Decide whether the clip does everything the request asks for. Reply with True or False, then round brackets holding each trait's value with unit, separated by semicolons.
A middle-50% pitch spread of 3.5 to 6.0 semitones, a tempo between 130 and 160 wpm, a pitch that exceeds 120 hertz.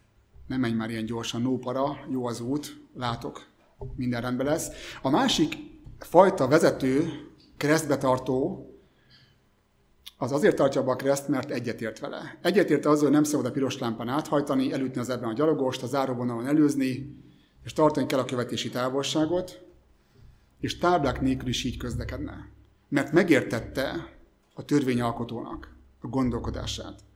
True (3.8 semitones; 140 wpm; 130 Hz)